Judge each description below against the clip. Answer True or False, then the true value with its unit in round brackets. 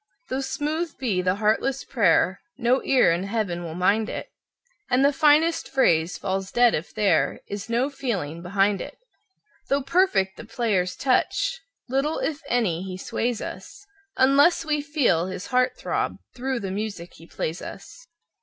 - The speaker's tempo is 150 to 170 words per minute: True (160 wpm)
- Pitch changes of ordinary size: False (6.4 semitones)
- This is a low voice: False (230 Hz)